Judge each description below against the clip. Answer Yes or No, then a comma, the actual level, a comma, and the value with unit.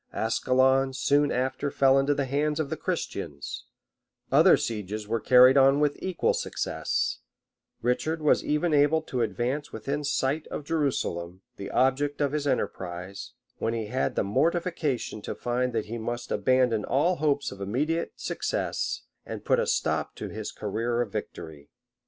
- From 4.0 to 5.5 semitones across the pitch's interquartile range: Yes, average, 4.5 semitones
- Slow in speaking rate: No, average, 165 wpm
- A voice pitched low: Yes, low, 130 Hz